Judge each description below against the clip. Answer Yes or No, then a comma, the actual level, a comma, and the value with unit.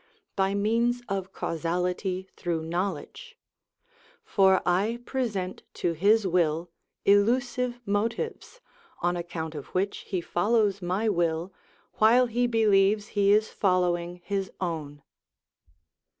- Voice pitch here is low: No, high, 195 Hz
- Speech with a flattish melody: No, average, 3.8 semitones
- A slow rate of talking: Yes, slow, 115 wpm